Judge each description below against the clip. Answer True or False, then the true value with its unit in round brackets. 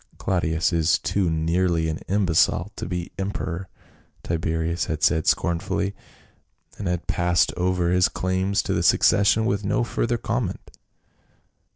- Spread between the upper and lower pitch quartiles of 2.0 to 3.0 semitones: True (2.7 semitones)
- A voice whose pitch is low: True (90 Hz)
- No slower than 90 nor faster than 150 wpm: True (140 wpm)